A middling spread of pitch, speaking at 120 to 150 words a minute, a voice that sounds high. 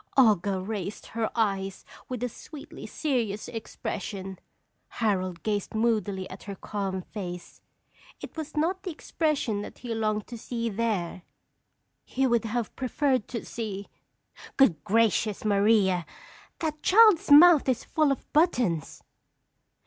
Yes: average, 5.0 semitones; slow, 135 wpm; high, 220 Hz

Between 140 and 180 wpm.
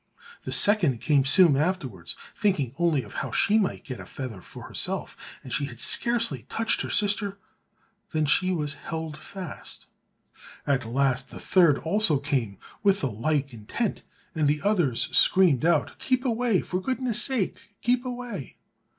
Yes: average, 160 wpm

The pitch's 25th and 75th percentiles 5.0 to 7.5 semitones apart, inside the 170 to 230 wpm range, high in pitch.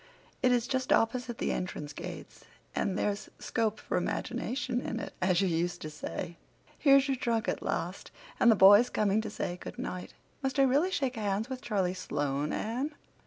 Yes: wide, 5.6 semitones; average, 180 wpm; high, 220 Hz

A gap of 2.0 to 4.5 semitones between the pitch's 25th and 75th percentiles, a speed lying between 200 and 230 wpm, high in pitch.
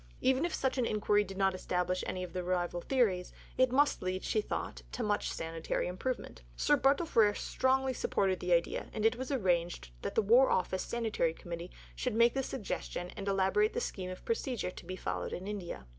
No: wide, 5.6 semitones; fast, 205 wpm; high, 200 Hz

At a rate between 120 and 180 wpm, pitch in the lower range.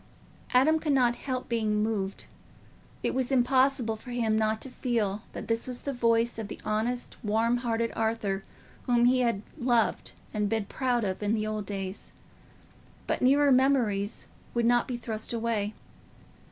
No: average, 160 wpm; high, 230 Hz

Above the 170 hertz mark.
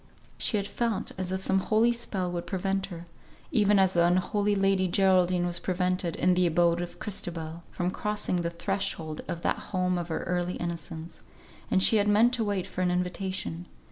Yes: medium, 185 Hz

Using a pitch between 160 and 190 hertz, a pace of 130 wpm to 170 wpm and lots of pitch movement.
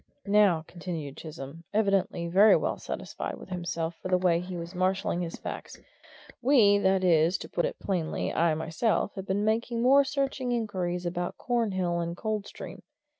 No: medium, 185 Hz; average, 165 wpm; average, 3.6 semitones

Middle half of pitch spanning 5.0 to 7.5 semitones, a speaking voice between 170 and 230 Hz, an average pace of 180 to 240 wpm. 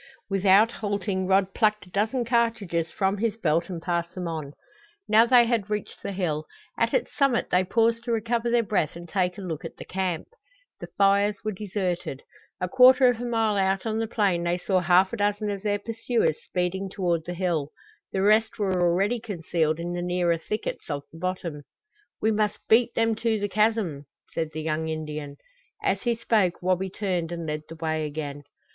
No: average, 4.2 semitones; high, 190 Hz; average, 195 wpm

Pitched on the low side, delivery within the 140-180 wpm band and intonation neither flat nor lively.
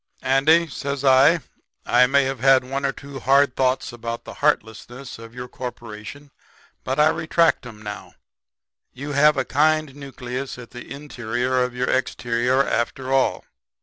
No: low, 130 Hz; average, 155 wpm; narrow, 2.3 semitones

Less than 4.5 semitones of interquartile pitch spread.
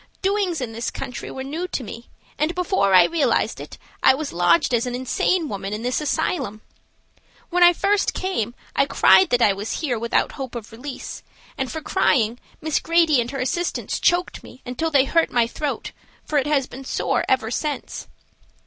No: wide, 5.5 semitones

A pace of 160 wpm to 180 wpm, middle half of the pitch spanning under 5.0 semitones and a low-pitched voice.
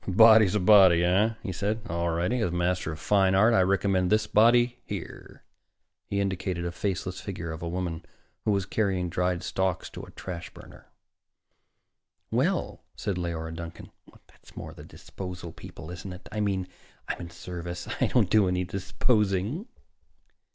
Yes: average, 170 wpm; average, 2.9 semitones; very low, 95 Hz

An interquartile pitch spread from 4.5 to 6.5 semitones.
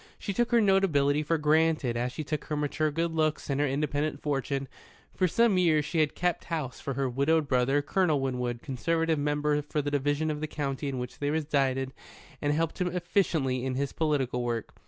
No: average, 2.8 semitones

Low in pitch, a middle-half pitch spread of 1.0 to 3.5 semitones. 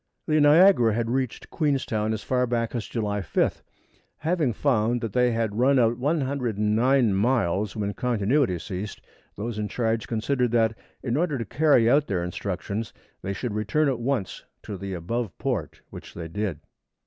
No: low, 115 Hz; average, 4.0 semitones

